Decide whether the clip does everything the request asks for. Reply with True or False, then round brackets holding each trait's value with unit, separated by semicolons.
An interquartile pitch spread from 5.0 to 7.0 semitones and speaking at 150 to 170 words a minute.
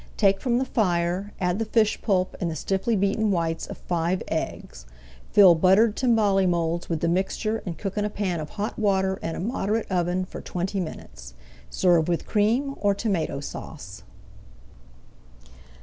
False (3.5 semitones; 165 wpm)